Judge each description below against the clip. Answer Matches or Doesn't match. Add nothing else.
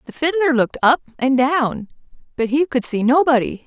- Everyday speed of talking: Matches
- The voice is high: Matches